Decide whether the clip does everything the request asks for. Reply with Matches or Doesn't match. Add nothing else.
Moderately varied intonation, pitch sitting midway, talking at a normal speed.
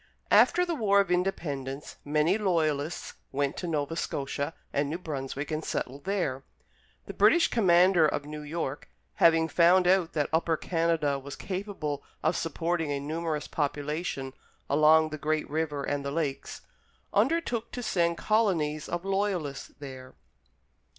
Matches